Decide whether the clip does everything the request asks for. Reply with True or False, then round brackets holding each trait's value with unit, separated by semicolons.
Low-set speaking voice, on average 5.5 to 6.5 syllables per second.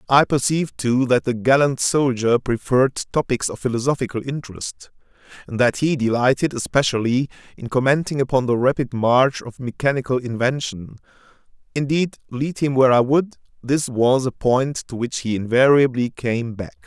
False (130 Hz; 5.1 syllables/s)